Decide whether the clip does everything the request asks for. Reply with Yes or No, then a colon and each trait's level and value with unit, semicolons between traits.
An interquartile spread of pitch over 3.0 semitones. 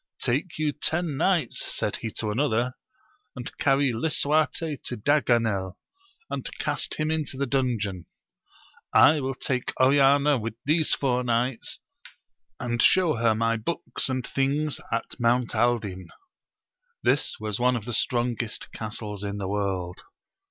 Yes: average, 4.1 semitones